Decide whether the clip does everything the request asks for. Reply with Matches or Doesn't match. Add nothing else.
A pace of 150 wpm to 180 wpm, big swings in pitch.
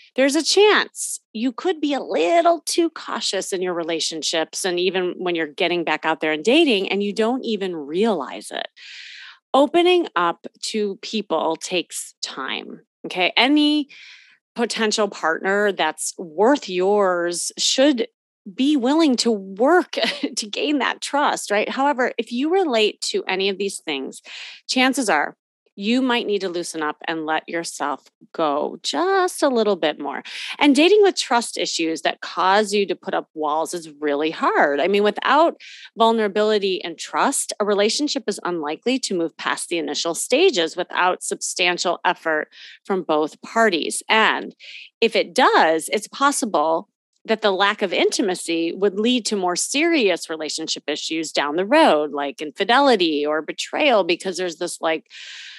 Matches